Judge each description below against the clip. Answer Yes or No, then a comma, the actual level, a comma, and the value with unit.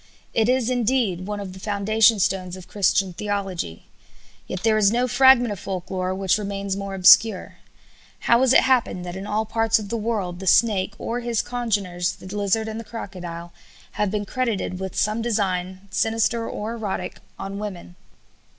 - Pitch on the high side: Yes, high, 205 Hz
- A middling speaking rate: Yes, average, 180 wpm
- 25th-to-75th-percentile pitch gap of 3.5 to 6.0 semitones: No, average, 3.1 semitones